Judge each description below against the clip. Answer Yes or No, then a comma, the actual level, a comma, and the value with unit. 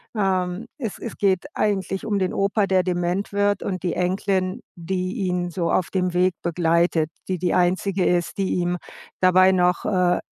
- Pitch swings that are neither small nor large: No, narrow, 1.5 semitones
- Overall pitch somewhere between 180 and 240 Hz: Yes, medium, 185 Hz